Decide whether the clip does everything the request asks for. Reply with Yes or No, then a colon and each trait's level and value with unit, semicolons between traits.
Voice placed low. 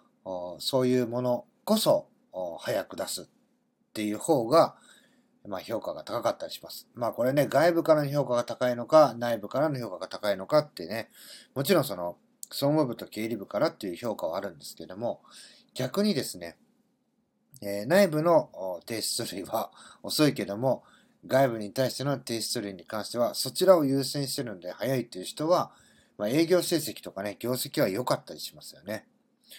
Yes: low, 130 Hz